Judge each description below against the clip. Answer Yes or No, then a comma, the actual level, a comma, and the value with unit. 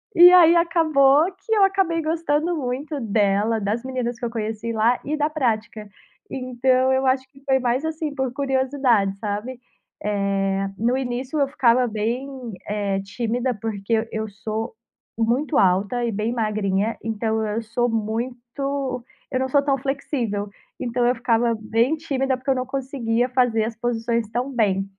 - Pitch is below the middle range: No, high, 245 Hz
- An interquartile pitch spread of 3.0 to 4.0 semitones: Yes, average, 3.5 semitones